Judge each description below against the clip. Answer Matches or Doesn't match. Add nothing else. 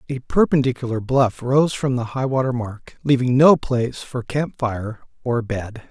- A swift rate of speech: Doesn't match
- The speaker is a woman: Doesn't match